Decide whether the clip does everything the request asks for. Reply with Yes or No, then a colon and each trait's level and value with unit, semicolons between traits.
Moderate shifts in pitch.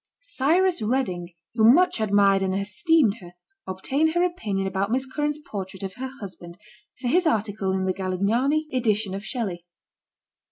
No: wide, 6.2 semitones